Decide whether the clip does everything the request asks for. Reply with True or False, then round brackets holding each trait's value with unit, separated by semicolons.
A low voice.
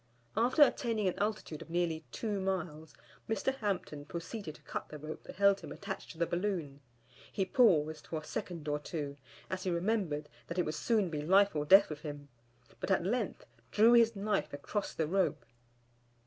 False (180 Hz)